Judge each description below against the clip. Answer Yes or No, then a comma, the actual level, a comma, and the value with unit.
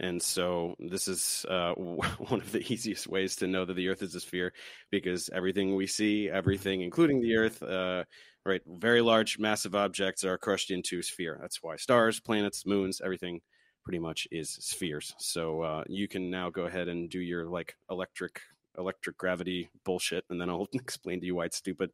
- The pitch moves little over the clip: Yes, narrow, 2.0 semitones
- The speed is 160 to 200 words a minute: Yes, average, 195 wpm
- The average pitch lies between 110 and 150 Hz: No, very low, 95 Hz